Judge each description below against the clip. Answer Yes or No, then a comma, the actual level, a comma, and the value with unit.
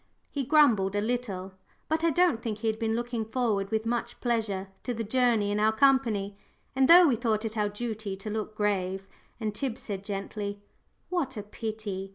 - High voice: Yes, high, 220 Hz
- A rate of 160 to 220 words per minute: Yes, average, 195 wpm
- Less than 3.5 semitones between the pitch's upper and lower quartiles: Yes, average, 3.0 semitones